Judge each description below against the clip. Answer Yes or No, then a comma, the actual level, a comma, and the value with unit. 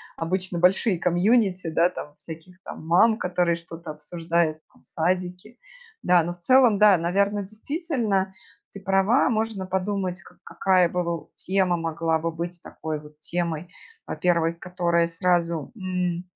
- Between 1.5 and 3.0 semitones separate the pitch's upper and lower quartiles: Yes, narrow, 2.4 semitones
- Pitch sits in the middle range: Yes, medium, 180 Hz